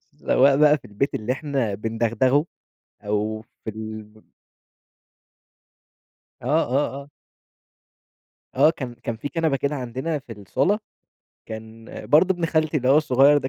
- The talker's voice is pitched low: Yes, low, 130 Hz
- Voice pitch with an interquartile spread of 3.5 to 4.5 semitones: No, average, 4.9 semitones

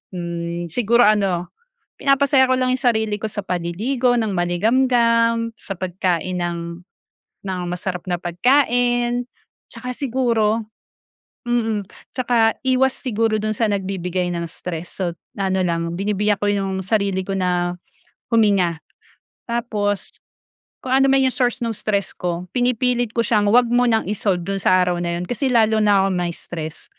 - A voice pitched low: No, high, 210 Hz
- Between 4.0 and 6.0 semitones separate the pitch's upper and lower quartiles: Yes, average, 5.0 semitones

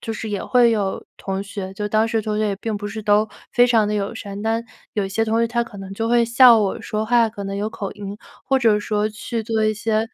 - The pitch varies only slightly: Yes, narrow, 1.8 semitones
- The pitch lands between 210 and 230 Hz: Yes, high, 215 Hz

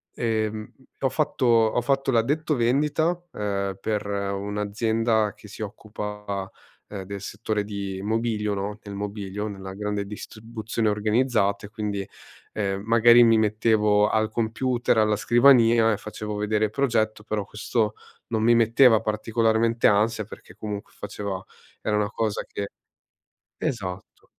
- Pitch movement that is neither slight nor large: No, narrow, 2.0 semitones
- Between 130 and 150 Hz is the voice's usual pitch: No, low, 110 Hz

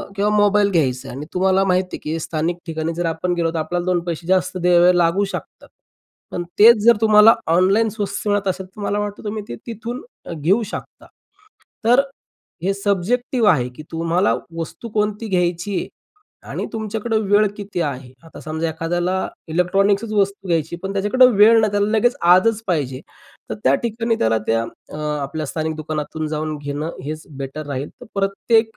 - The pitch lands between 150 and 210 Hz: Yes, medium, 185 Hz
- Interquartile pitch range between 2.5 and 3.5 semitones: No, average, 4.4 semitones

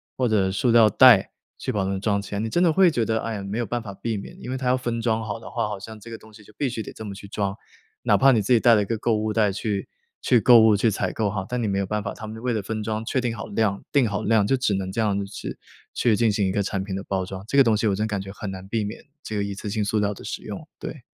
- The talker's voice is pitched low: Yes, low, 110 Hz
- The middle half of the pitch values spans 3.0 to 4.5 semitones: No, narrow, 2.4 semitones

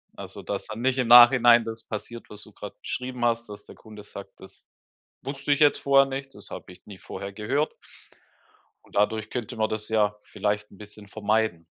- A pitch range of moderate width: Yes, average, 3.2 semitones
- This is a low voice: Yes, low, 110 Hz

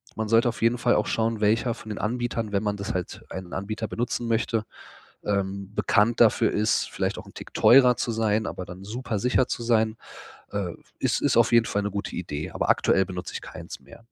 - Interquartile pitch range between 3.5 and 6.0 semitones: No, narrow, 2.6 semitones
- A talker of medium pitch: No, low, 110 Hz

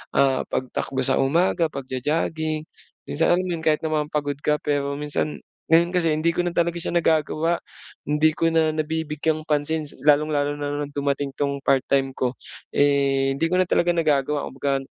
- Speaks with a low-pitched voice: No, medium, 150 Hz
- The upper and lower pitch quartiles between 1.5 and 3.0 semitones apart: Yes, narrow, 2.4 semitones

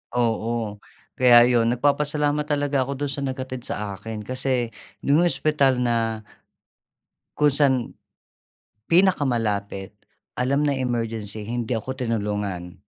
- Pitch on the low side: Yes, low, 125 Hz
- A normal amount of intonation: Yes, average, 3.8 semitones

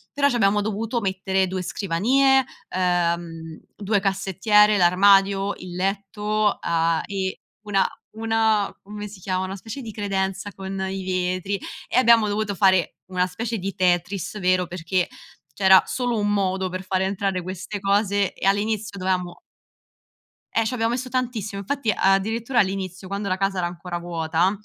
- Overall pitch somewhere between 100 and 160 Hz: No, high, 195 Hz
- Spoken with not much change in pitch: Yes, narrow, 2.3 semitones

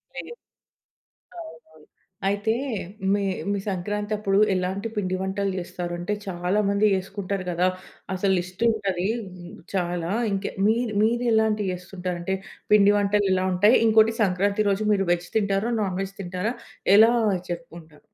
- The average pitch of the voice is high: Yes, high, 195 Hz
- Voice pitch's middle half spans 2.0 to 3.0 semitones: Yes, narrow, 2.5 semitones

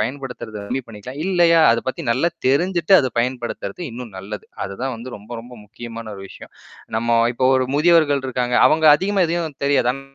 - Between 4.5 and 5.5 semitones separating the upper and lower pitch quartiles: Yes, average, 5.0 semitones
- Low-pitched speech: Yes, low, 130 Hz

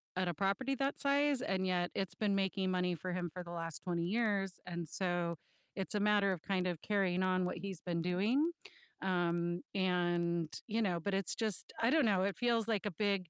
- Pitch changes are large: No, average, 2.8 semitones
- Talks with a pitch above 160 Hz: Yes, medium, 185 Hz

